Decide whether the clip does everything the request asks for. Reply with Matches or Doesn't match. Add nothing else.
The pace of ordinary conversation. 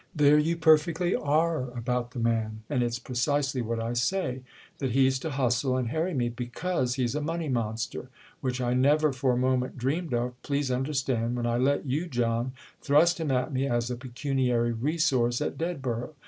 Matches